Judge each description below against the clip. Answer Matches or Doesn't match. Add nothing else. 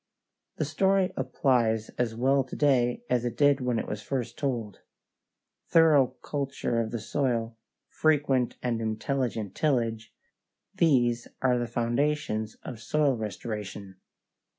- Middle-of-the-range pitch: Doesn't match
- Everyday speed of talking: Doesn't match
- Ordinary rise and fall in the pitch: Matches